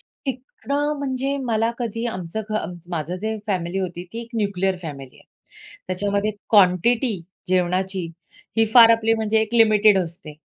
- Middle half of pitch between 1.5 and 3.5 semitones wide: No, average, 3.9 semitones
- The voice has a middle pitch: No, high, 205 Hz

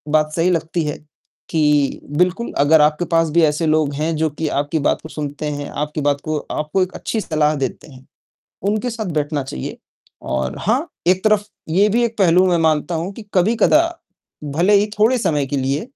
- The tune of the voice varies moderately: Yes, average, 4.1 semitones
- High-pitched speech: No, medium, 160 Hz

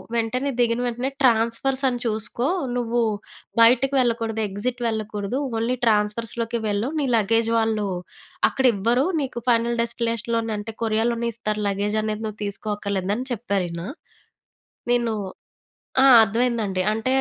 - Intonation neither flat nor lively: No, narrow, 2.1 semitones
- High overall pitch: Yes, high, 230 Hz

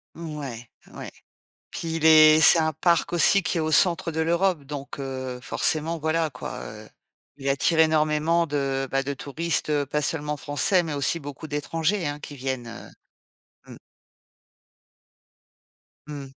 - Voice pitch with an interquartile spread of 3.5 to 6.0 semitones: No, average, 2.8 semitones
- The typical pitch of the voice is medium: Yes, medium, 150 Hz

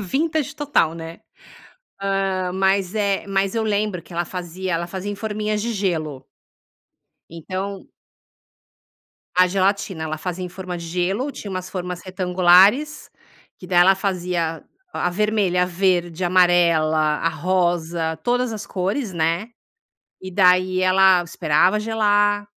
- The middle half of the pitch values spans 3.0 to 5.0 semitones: No, narrow, 2.5 semitones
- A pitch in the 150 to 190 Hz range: Yes, medium, 185 Hz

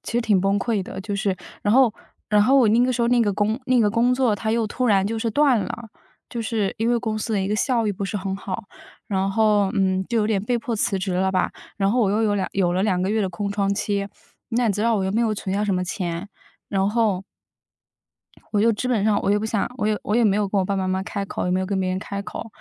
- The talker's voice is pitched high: Yes, high, 205 Hz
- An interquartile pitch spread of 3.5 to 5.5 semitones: No, average, 2.7 semitones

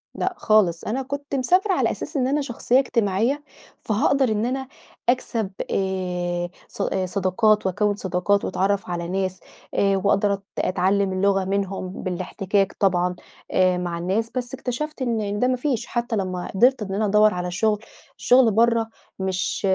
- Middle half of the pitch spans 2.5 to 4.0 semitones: No, average, 4.4 semitones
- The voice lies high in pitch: Yes, high, 205 Hz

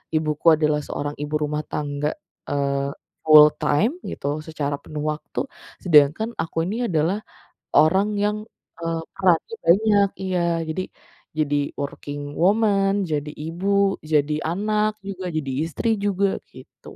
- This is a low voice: No, medium, 160 Hz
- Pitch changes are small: No, average, 4.8 semitones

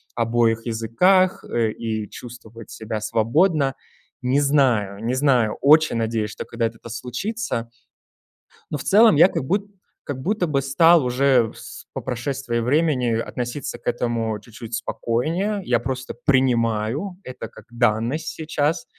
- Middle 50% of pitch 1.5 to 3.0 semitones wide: No, average, 4.5 semitones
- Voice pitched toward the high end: No, low, 125 Hz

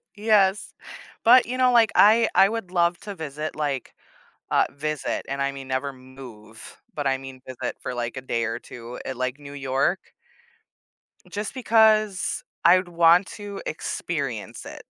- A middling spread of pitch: No, wide, 7.4 semitones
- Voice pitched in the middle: Yes, medium, 150 Hz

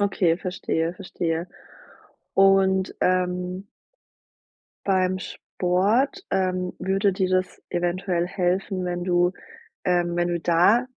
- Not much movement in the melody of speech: Yes, narrow, 1.5 semitones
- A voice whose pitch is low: No, medium, 185 Hz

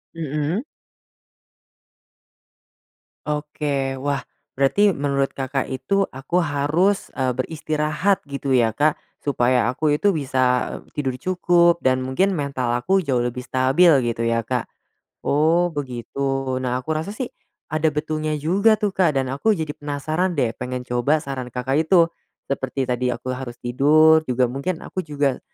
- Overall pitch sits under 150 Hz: Yes, medium, 140 Hz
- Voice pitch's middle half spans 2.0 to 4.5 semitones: Yes, average, 3.5 semitones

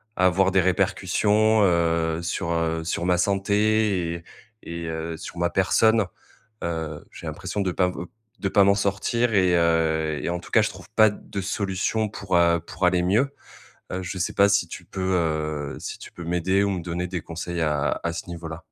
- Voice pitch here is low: Yes, very low, 90 Hz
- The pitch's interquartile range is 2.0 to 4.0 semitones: Yes, average, 2.9 semitones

